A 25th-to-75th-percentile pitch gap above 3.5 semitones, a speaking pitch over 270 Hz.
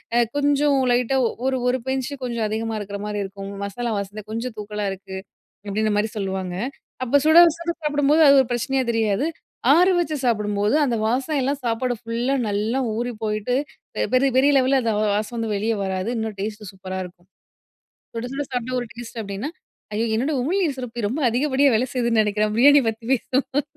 No: average, 4.1 semitones; high, 235 Hz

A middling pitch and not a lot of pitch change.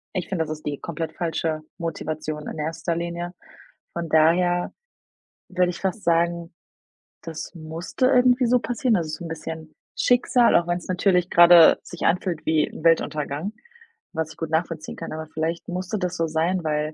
Yes: medium, 170 Hz; narrow, 2.2 semitones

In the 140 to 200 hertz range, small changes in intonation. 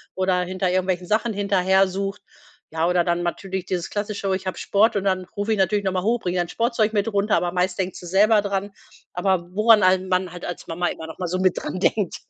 Yes: high, 190 Hz; narrow, 2.1 semitones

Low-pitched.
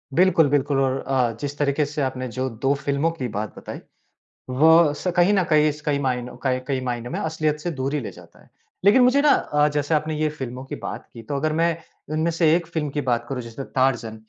No: medium, 145 Hz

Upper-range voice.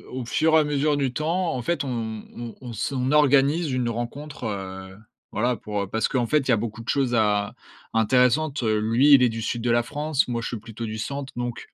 No: low, 125 Hz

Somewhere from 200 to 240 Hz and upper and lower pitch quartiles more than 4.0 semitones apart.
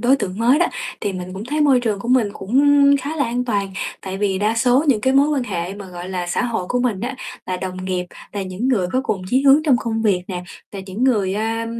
Yes: high, 220 Hz; average, 5.1 semitones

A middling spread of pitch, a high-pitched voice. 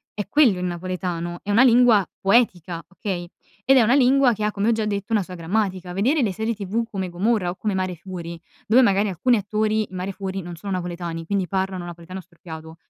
Yes: average, 3.5 semitones; high, 195 Hz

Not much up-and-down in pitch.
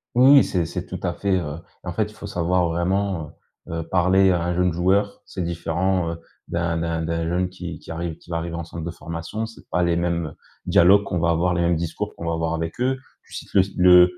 Yes: narrow, 1.8 semitones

